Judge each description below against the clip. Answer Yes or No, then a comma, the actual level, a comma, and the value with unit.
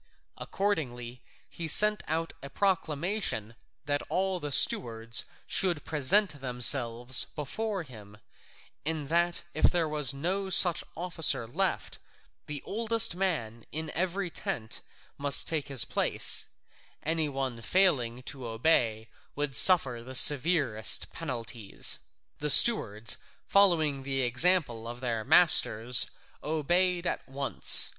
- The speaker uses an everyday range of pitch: No, wide, 6.3 semitones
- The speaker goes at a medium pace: No, slow, 115 wpm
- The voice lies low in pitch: No, medium, 145 Hz